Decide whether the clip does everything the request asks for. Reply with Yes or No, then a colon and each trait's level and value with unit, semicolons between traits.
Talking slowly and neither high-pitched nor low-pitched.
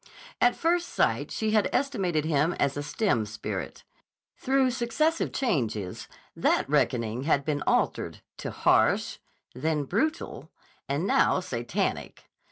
Yes: slow, 125 wpm; medium, 165 Hz